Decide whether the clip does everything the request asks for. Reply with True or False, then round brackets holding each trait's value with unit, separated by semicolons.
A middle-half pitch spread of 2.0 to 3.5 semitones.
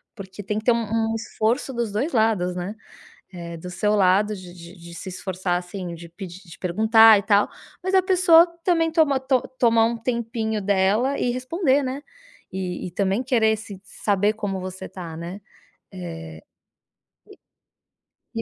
False (4.6 semitones)